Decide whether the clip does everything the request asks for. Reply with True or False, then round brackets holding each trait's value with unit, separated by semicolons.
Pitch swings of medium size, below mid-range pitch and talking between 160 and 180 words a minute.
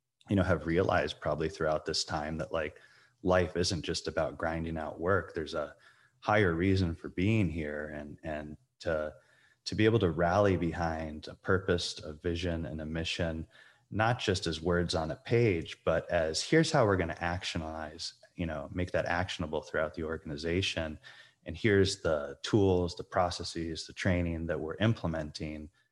True (3.4 semitones; 85 Hz; 170 wpm)